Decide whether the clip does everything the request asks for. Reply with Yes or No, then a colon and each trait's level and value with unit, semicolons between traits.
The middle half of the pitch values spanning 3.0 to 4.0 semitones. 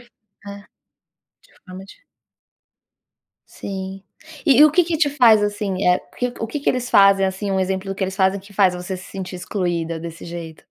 No: narrow, 2.4 semitones